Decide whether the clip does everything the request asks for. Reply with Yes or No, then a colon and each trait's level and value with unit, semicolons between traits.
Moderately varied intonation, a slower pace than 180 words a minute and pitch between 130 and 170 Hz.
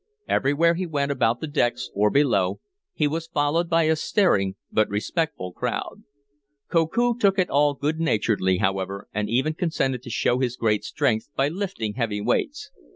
No: wide, 7.3 semitones; average, 165 wpm; medium, 140 Hz